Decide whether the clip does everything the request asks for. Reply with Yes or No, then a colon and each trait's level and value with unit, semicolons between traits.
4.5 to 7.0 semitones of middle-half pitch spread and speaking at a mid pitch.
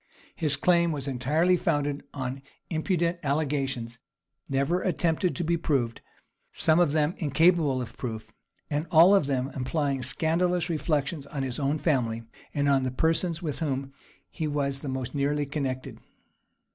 No: average, 3.5 semitones; medium, 145 Hz